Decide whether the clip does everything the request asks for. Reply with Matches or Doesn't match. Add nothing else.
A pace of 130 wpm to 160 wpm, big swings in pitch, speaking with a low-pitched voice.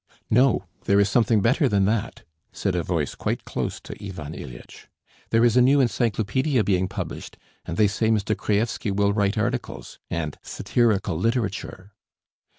Doesn't match